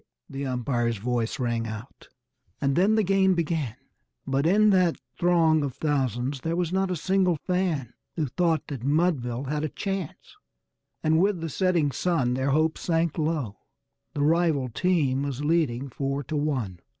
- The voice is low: No, medium, 150 Hz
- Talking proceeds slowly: No, average, 160 wpm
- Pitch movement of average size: Yes, average, 4.7 semitones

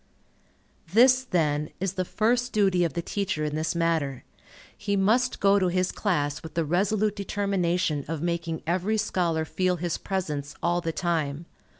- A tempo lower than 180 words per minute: Yes, average, 165 wpm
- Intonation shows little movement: No, average, 3.8 semitones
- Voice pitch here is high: No, medium, 175 Hz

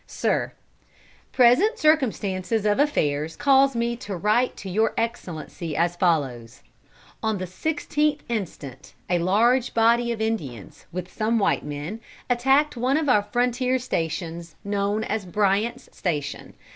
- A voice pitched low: No, high, 215 Hz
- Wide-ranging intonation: Yes, wide, 6.0 semitones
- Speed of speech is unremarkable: No, slow, 130 wpm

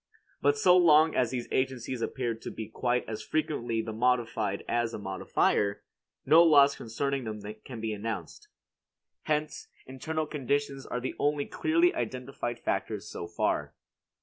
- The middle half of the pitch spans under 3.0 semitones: No, average, 4.5 semitones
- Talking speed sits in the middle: Yes, average, 150 wpm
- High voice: No, low, 125 Hz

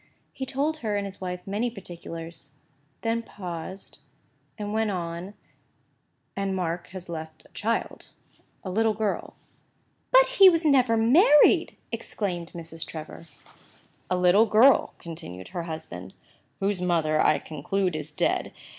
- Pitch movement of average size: Yes, average, 5.0 semitones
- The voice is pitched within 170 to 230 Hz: Yes, medium, 185 Hz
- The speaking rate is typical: No, slow, 120 wpm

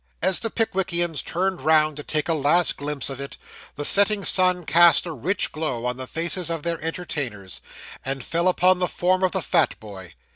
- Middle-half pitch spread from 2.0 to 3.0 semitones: No, average, 4.1 semitones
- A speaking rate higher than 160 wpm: Yes, average, 195 wpm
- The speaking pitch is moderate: Yes, medium, 165 Hz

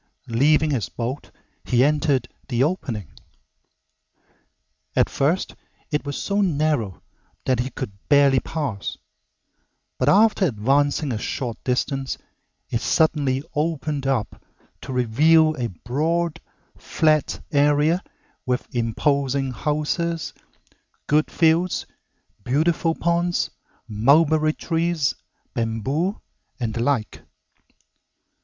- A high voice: No, medium, 145 Hz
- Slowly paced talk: Yes, slow, 100 wpm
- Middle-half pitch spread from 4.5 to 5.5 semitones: No, average, 4.1 semitones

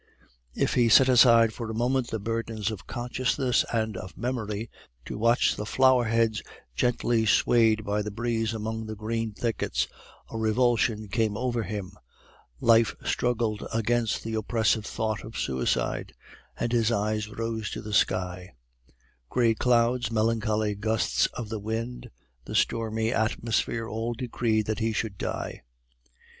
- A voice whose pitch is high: No, low, 115 Hz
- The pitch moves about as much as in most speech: No, narrow, 1.6 semitones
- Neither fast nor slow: Yes, average, 145 wpm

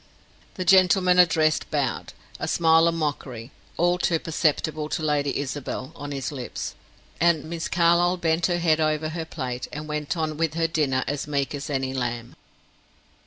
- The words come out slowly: No, average, 165 wpm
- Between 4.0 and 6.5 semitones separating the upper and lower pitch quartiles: No, average, 2.9 semitones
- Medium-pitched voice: Yes, medium, 155 Hz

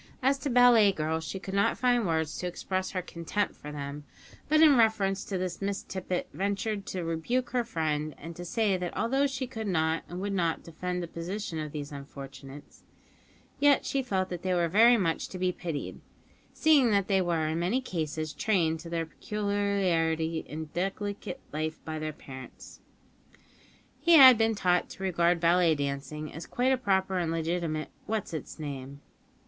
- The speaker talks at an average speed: Yes, average, 180 wpm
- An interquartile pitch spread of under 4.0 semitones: No, average, 4.4 semitones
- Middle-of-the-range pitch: Yes, medium, 180 Hz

